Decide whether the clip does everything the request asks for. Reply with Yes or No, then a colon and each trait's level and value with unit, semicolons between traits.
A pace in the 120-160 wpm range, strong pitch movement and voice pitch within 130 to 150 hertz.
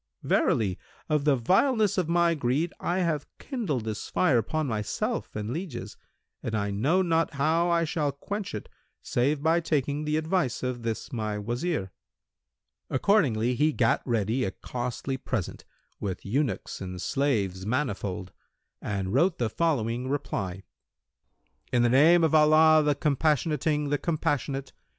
Yes: average, 145 wpm; wide, 5.7 semitones; medium, 140 Hz